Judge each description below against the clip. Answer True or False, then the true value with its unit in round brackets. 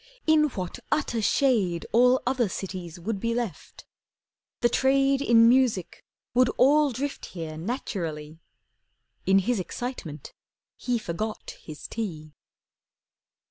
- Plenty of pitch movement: True (6.3 semitones)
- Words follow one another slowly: True (115 wpm)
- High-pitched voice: True (230 Hz)